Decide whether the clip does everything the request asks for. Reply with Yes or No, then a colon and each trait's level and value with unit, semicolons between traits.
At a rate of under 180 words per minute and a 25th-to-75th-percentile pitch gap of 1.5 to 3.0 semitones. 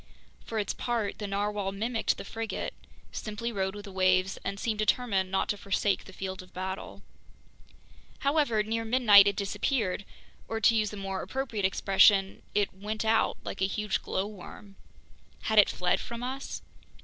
Yes: average, 165 wpm; narrow, 2.6 semitones